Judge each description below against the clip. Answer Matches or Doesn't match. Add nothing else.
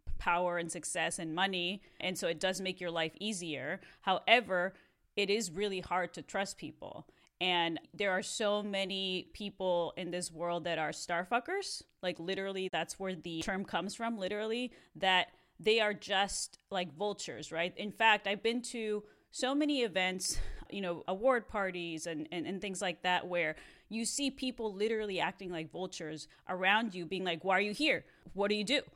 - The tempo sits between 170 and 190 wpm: Matches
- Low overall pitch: Doesn't match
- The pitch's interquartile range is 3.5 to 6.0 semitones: Doesn't match